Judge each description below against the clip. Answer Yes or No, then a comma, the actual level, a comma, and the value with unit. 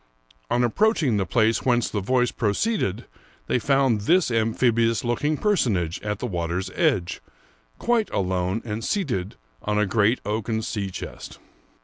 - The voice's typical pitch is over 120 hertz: No, low, 115 Hz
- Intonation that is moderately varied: Yes, average, 4.1 semitones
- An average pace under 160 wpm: Yes, average, 145 wpm